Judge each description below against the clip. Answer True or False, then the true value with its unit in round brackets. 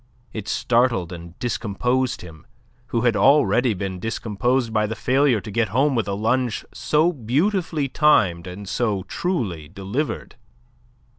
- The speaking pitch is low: True (115 Hz)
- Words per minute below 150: True (140 wpm)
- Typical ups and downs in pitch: True (4.8 semitones)